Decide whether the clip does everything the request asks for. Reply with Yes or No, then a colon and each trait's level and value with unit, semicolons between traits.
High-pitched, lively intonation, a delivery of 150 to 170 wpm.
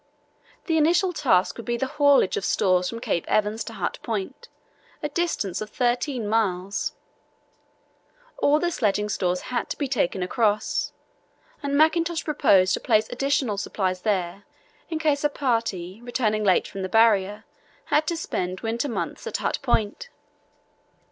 Yes: high, 225 Hz; wide, 6.4 semitones; average, 155 wpm